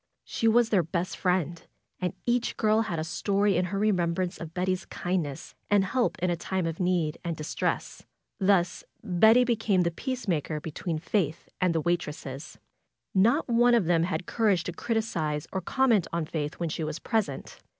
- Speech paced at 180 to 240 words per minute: Yes, average, 185 wpm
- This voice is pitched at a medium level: Yes, medium, 180 Hz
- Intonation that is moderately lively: Yes, average, 4.3 semitones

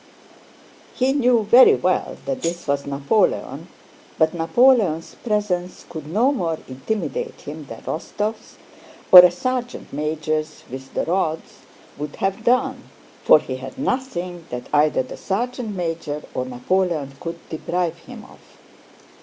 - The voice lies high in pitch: No, medium, 175 Hz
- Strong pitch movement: Yes, wide, 6.6 semitones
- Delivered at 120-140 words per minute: Yes, slow, 135 wpm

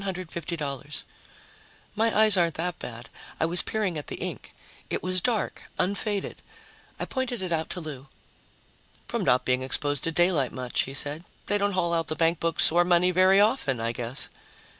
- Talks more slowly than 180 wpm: Yes, average, 170 wpm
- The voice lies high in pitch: No, medium, 170 Hz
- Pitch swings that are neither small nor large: Yes, average, 4.7 semitones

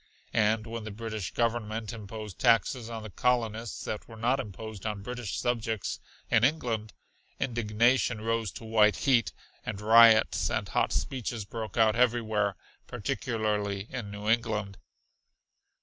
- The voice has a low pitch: Yes, low, 110 Hz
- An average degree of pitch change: No, narrow, 1.7 semitones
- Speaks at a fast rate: No, slow, 135 wpm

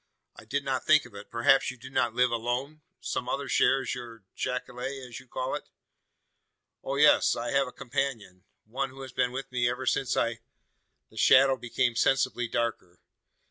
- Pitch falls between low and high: No, low, 125 Hz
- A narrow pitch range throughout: Yes, narrow, 2.2 semitones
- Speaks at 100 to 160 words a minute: No, average, 185 wpm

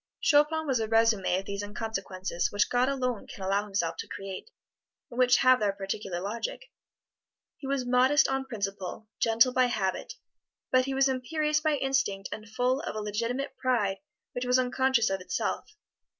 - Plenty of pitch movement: No, average, 4.8 semitones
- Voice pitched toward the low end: No, high, 235 Hz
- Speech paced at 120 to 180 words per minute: Yes, average, 170 wpm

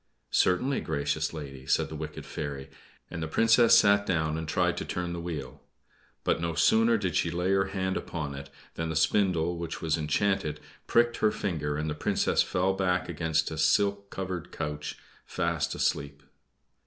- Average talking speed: Yes, average, 175 wpm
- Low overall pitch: Yes, very low, 85 Hz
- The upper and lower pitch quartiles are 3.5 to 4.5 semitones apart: Yes, average, 3.9 semitones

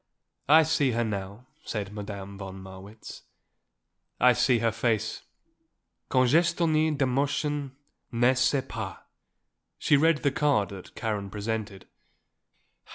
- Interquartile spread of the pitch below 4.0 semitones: No, wide, 5.6 semitones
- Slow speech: Yes, slow, 110 wpm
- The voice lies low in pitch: Yes, low, 115 Hz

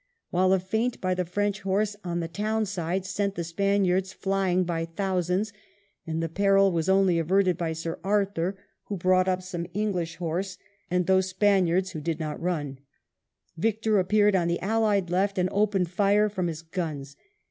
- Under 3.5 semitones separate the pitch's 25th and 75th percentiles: Yes, average, 2.7 semitones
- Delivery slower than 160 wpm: No, average, 180 wpm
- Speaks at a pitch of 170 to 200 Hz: Yes, medium, 185 Hz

